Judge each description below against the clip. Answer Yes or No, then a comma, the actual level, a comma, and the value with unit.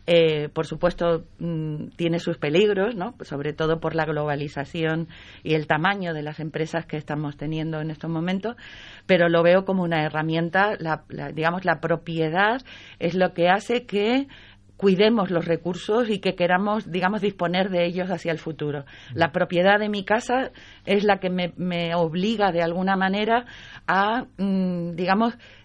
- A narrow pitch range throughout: No, average, 3.4 semitones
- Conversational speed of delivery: Yes, average, 165 wpm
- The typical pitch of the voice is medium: Yes, medium, 170 Hz